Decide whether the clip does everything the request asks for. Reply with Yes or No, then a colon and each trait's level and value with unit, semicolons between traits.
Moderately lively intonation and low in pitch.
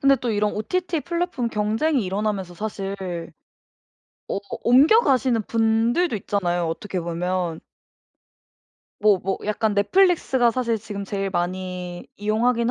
No: average, 4.3 semitones; high, 215 Hz